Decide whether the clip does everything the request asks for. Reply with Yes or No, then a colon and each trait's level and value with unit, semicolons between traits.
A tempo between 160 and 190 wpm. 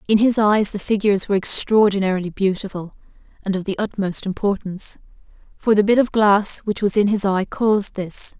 Yes: average, 180 wpm